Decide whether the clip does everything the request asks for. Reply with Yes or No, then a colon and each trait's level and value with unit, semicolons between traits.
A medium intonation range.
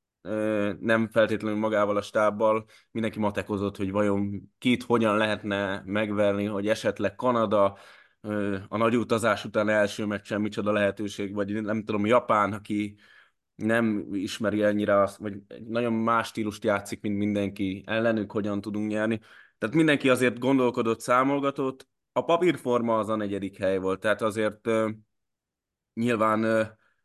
No: narrow, 1.8 semitones